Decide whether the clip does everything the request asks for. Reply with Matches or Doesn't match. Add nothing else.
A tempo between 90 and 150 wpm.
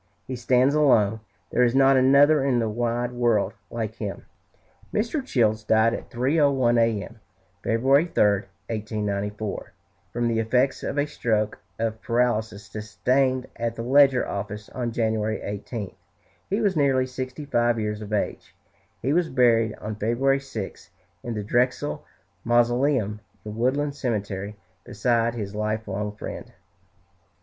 Matches